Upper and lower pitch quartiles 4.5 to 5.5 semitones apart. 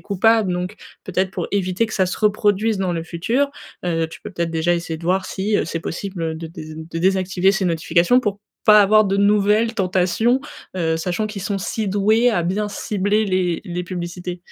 No: average, 3.2 semitones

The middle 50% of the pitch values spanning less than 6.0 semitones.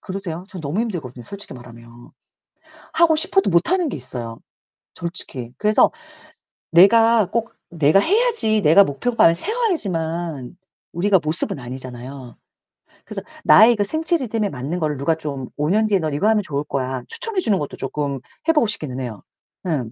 No: wide, 8.2 semitones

